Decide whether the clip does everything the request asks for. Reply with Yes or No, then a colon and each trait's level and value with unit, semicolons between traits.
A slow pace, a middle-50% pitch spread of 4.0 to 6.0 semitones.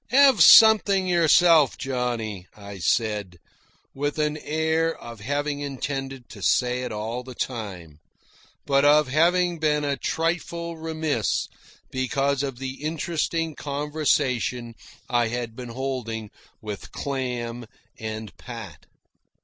Yes: slow, 115 wpm; average, 4.9 semitones